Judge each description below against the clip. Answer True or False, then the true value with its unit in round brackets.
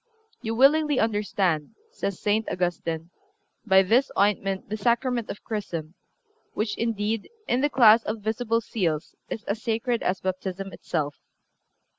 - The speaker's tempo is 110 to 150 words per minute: True (140 wpm)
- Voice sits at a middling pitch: False (210 Hz)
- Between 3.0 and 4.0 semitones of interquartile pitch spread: True (3.5 semitones)